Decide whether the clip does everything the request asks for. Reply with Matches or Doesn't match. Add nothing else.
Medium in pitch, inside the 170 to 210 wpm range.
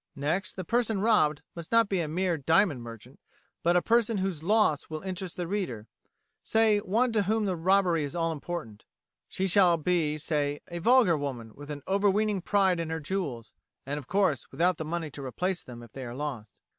Matches